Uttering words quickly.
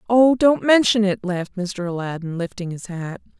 No: average, 175 wpm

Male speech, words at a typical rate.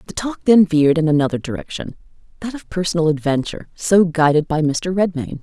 No: female; average, 165 wpm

